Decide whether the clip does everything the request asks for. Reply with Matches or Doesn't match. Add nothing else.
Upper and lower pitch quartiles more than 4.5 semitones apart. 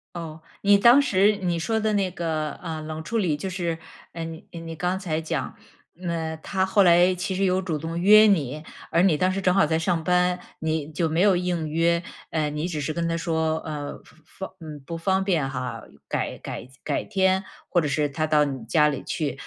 Doesn't match